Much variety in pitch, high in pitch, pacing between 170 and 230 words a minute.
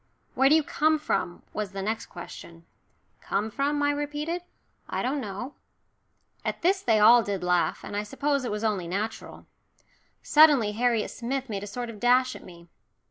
Yes: wide, 5.8 semitones; high, 235 Hz; average, 180 wpm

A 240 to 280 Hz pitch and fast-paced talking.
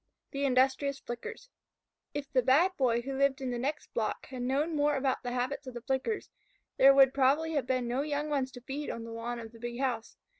Yes: very high, 265 Hz; fast, 220 wpm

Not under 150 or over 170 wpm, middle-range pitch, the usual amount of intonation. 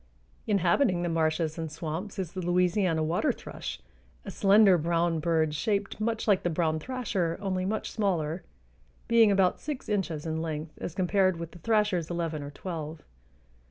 Yes: average, 160 wpm; medium, 175 Hz; average, 3.7 semitones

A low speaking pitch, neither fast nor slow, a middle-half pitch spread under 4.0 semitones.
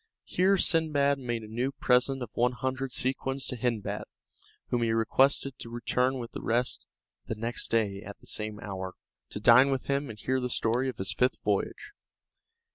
Yes: low, 125 Hz; average, 180 wpm; average, 2.9 semitones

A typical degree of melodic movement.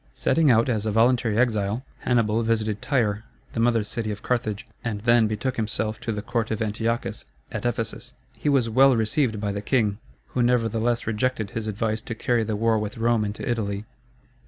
No: narrow, 2.0 semitones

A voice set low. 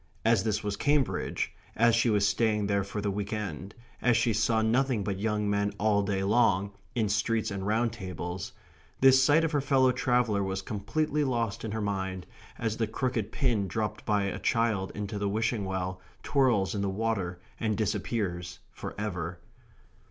Yes: low, 105 Hz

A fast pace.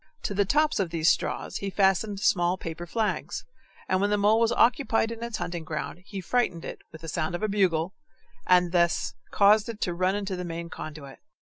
Yes: fast, 210 wpm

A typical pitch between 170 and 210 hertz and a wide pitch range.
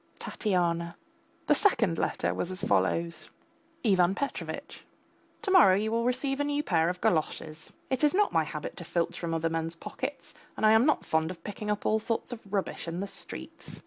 Yes: high, 190 Hz; wide, 5.9 semitones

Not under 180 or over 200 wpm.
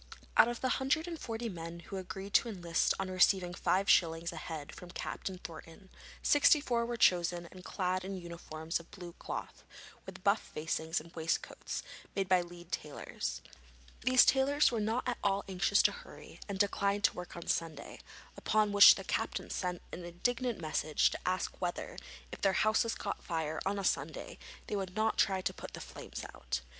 Yes: average, 185 wpm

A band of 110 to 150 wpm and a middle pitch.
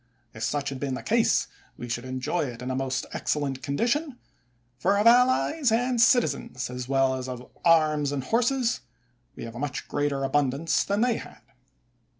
No: average, 175 wpm; medium, 145 Hz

